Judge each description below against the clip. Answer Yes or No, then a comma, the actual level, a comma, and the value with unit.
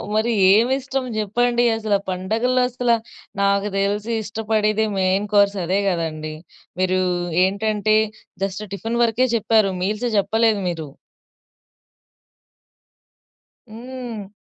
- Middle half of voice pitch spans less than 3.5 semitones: Yes, average, 2.8 semitones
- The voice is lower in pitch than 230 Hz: Yes, high, 215 Hz